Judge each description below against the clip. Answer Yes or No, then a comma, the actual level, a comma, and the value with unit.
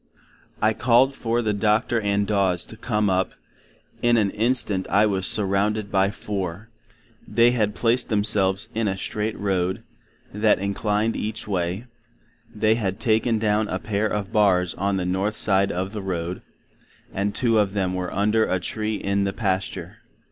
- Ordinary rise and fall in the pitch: No, narrow, 2.3 semitones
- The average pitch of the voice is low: Yes, low, 105 Hz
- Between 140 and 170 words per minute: Yes, average, 160 wpm